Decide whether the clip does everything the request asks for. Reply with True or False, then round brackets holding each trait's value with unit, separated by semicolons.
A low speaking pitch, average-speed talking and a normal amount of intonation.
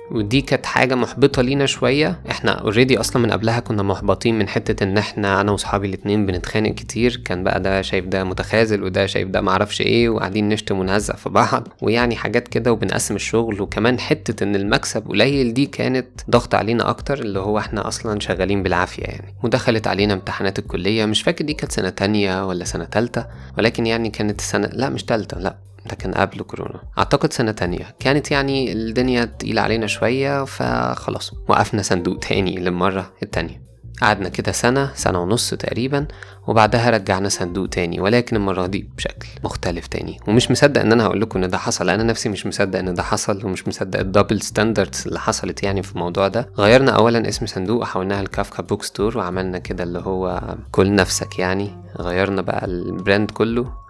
False (105 Hz; 180 wpm; 3.4 semitones)